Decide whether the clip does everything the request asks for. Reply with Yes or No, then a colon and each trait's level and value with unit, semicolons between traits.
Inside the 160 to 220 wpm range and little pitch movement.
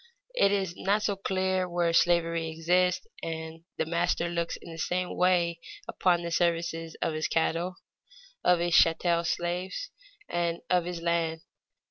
No: average, 150 wpm; narrow, 1.4 semitones